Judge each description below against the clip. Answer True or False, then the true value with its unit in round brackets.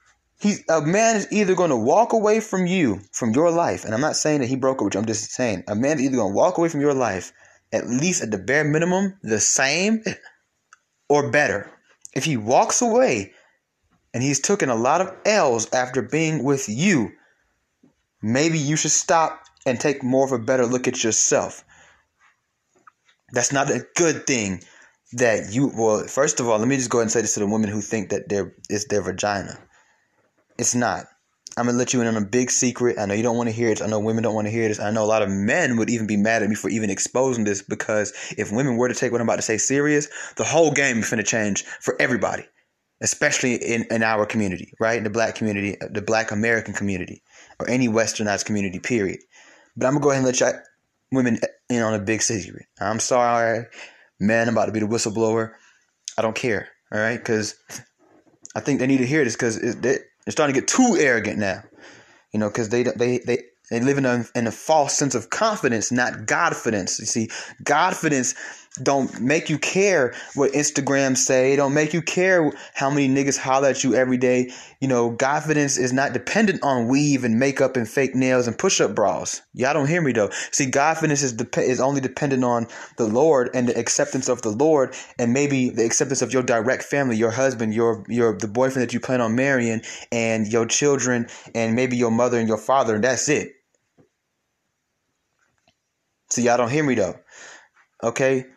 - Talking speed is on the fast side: True (215 wpm)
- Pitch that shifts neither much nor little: True (3.8 semitones)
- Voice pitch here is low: True (125 Hz)